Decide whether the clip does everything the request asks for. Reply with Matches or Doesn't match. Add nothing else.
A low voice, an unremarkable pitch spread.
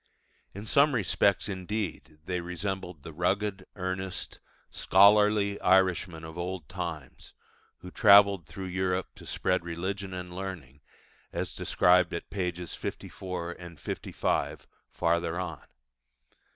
Doesn't match